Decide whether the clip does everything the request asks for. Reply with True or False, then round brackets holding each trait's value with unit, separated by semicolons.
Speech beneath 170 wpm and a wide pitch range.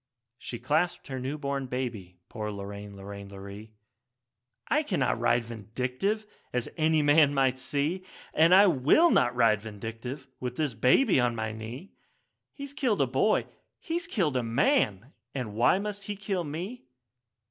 True (160 wpm; 7.6 semitones)